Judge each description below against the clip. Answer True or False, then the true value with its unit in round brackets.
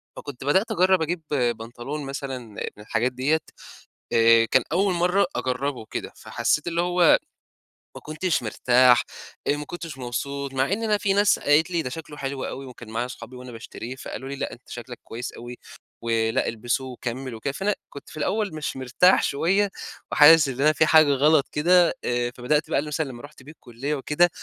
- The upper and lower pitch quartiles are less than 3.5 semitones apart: False (4.7 semitones)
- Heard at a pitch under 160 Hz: True (140 Hz)